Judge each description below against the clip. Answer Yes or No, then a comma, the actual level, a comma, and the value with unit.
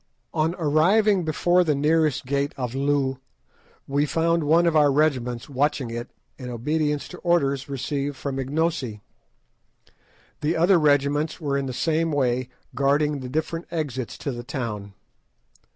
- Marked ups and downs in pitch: No, average, 3.2 semitones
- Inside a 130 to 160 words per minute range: Yes, average, 145 wpm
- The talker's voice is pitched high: No, medium, 145 Hz